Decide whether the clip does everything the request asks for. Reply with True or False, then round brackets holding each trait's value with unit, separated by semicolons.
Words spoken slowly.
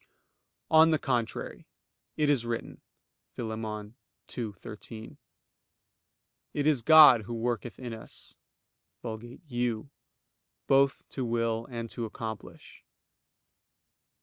True (95 wpm)